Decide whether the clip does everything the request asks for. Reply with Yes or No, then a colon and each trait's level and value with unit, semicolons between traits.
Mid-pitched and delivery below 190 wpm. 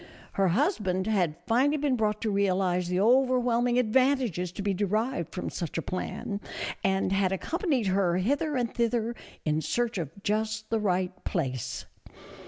No: high, 210 Hz; average, 155 wpm